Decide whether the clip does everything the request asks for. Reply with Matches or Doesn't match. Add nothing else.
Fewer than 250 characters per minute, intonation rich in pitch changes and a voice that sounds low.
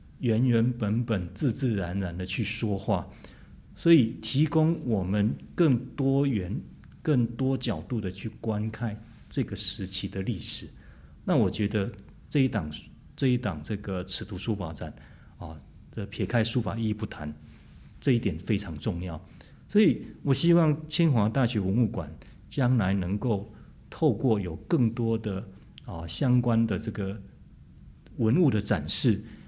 Doesn't match